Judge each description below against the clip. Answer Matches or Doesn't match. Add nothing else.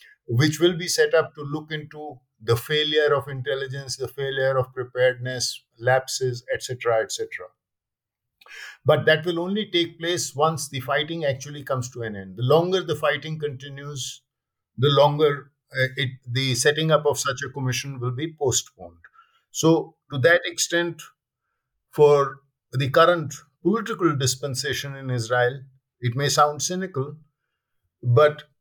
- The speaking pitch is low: Doesn't match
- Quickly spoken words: Doesn't match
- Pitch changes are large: Doesn't match